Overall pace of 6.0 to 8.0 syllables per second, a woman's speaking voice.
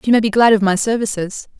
Yes: 6.4 syllables/s; female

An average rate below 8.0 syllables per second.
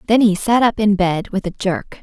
Yes: 4.9 syllables/s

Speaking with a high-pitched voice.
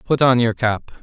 No: low, 120 Hz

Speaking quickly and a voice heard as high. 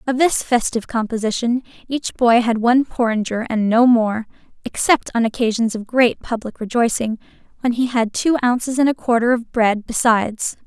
No: average, 165 wpm; high, 235 Hz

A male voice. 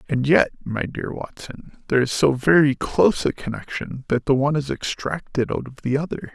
Yes: male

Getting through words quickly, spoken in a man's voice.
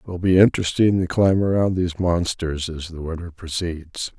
No: average, 185 wpm; male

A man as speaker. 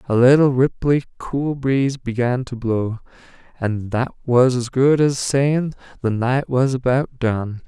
Yes: male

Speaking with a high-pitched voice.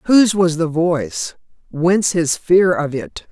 No: medium, 175 Hz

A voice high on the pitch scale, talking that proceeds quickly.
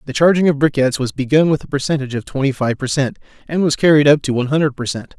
No: medium, 140 Hz; fast, 265 wpm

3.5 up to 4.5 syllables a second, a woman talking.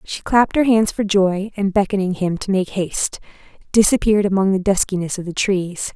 No: 5.5 syllables/s; female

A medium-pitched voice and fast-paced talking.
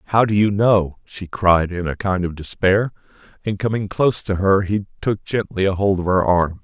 No: very low, 95 Hz; fast, 210 wpm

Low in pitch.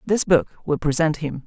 No: medium, 155 Hz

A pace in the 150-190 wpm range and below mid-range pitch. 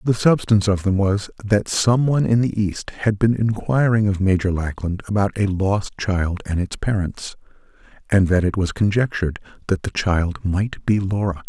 Yes: average, 185 wpm; low, 100 Hz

